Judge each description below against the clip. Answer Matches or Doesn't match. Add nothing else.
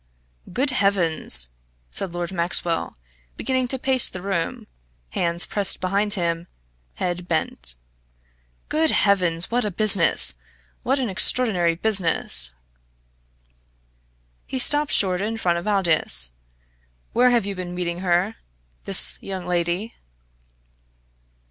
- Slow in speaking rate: Matches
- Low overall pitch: Doesn't match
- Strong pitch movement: Doesn't match